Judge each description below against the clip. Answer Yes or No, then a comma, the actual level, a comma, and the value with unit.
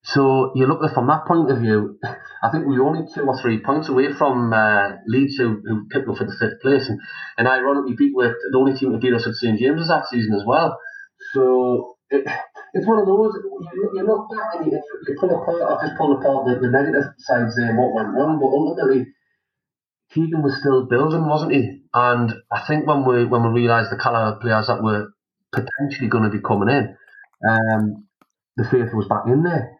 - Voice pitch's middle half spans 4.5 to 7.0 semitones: Yes, average, 4.8 semitones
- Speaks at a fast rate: Yes, fast, 215 wpm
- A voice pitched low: Yes, low, 130 Hz